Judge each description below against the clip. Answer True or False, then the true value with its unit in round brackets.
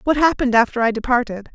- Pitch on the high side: True (250 Hz)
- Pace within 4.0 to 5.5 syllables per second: False (7.0 syllables/s)